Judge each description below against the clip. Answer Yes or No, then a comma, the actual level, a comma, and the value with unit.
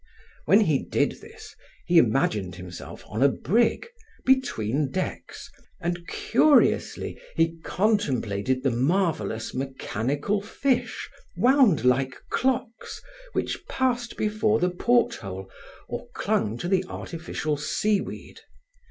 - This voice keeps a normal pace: No, slow, 110 wpm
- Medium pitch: Yes, medium, 165 Hz